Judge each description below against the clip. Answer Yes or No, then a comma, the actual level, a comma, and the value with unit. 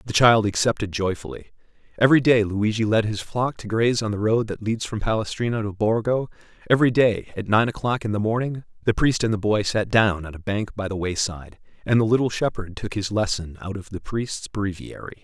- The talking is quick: Yes, fast, 215 wpm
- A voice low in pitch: Yes, low, 105 Hz